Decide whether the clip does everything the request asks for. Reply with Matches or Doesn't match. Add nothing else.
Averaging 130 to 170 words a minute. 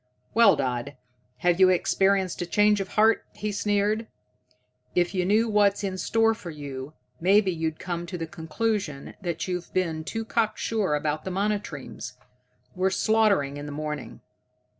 Matches